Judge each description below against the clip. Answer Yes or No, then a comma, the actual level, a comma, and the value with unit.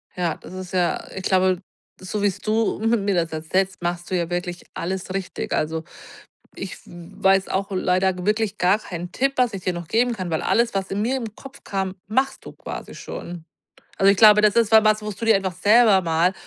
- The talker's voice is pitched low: No, high, 190 Hz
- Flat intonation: No, average, 3.0 semitones